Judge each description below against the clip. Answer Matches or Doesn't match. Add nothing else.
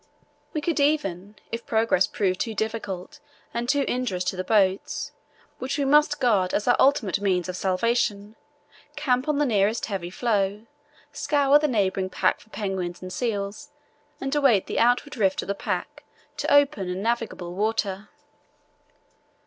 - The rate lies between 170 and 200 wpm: Doesn't match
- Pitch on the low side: Doesn't match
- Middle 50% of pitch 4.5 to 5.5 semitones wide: Matches